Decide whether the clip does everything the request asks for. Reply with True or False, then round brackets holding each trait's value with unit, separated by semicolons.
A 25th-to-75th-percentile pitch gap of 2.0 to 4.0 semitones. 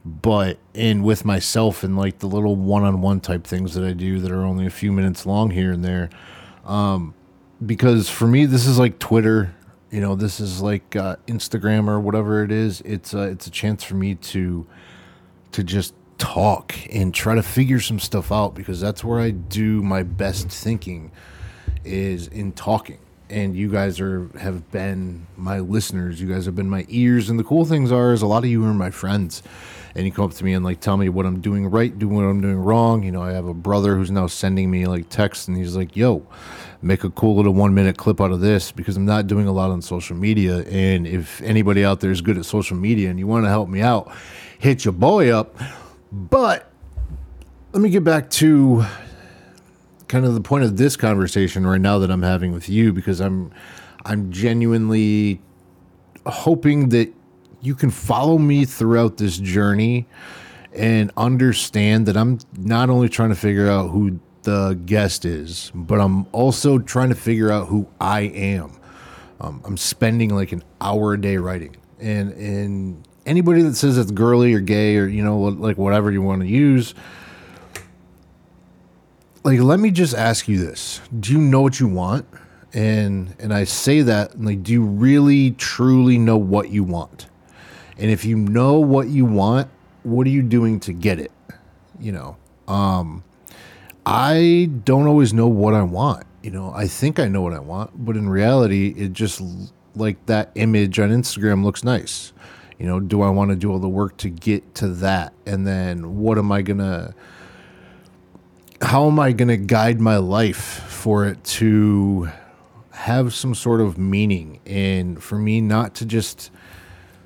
True (3.3 semitones)